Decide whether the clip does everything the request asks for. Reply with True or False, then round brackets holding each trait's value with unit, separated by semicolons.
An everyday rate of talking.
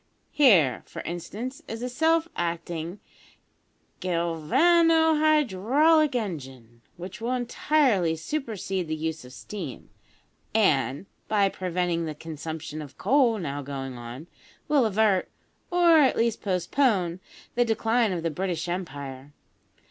False (120 wpm)